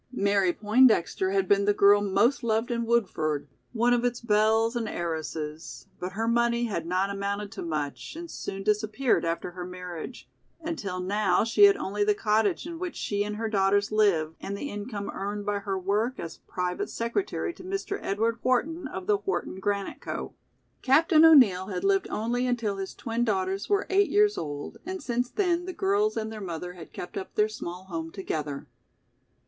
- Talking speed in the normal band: Yes, average, 185 wpm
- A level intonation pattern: No, average, 4.3 semitones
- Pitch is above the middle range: Yes, high, 210 Hz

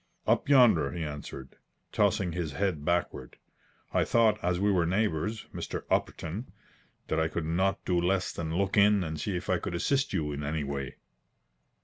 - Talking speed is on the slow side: No, average, 175 wpm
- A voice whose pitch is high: No, very low, 90 Hz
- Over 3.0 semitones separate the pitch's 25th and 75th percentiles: Yes, average, 4.1 semitones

